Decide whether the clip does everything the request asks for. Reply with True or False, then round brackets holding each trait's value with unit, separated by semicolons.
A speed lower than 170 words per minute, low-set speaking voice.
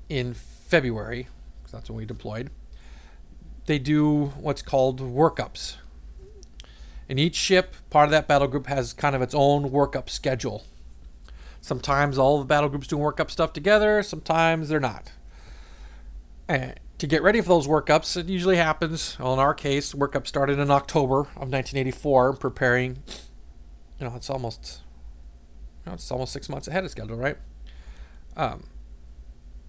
True (150 wpm; 130 Hz)